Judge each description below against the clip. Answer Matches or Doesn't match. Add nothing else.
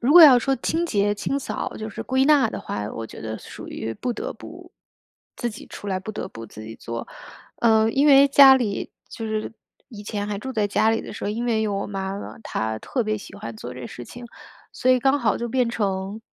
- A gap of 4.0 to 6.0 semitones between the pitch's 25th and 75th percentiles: Matches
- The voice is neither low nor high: Doesn't match